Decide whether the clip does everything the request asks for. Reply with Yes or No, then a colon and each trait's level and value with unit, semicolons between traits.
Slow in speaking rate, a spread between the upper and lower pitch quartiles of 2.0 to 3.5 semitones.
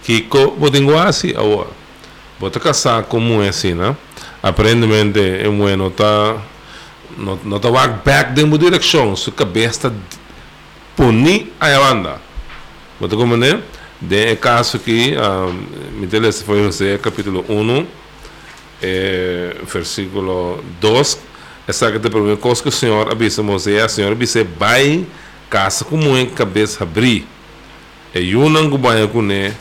No: slow, 90 wpm; average, 3.9 semitones